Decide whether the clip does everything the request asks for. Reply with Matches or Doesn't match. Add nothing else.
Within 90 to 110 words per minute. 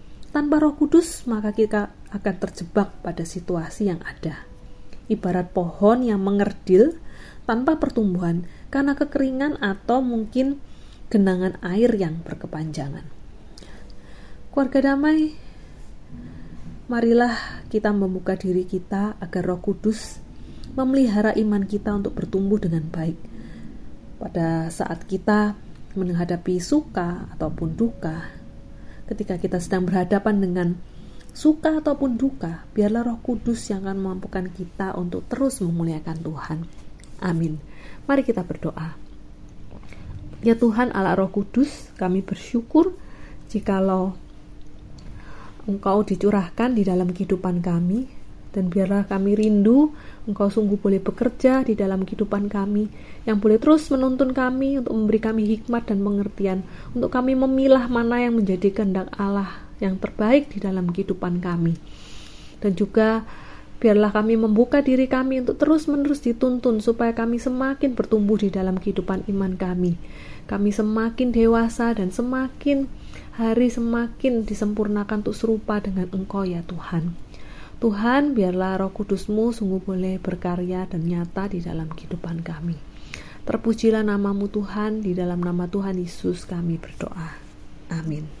Doesn't match